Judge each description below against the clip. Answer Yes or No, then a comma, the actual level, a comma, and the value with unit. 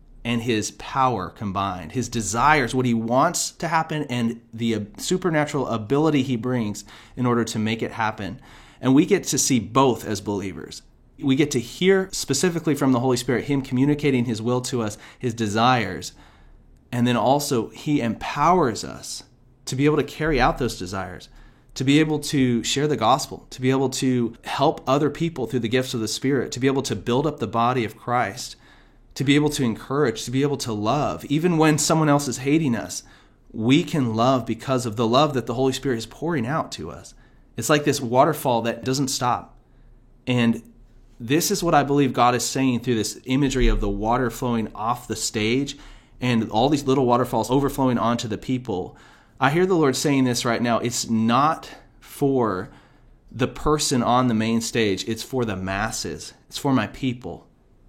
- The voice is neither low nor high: No, low, 125 Hz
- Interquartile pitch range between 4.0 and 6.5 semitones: No, average, 3.3 semitones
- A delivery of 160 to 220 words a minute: Yes, average, 190 wpm